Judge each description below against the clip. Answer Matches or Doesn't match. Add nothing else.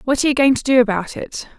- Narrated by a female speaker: Matches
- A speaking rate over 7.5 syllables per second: Doesn't match